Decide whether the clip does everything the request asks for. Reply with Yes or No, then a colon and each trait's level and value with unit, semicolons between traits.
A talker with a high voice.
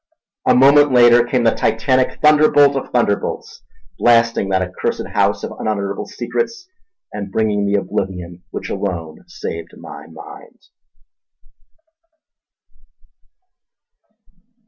No: low, 110 Hz